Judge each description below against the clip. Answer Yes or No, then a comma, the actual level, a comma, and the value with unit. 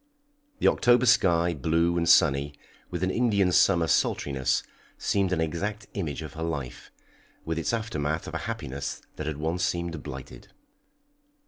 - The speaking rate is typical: Yes, average, 150 wpm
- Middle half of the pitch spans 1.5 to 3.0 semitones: No, average, 4.2 semitones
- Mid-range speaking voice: No, very low, 85 Hz